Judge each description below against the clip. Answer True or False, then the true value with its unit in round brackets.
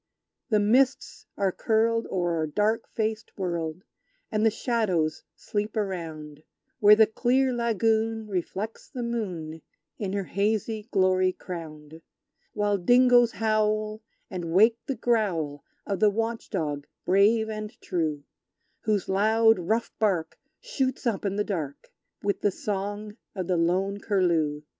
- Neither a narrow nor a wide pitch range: True (3.8 semitones)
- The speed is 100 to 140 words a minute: True (135 wpm)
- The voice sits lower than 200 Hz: False (205 Hz)